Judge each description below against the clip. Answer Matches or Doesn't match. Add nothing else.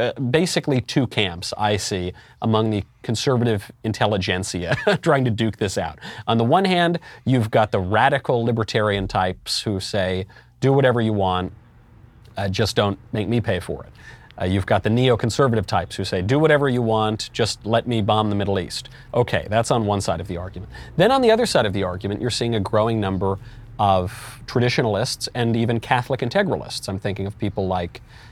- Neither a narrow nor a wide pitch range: Matches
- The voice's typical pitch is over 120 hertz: Doesn't match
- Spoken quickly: Doesn't match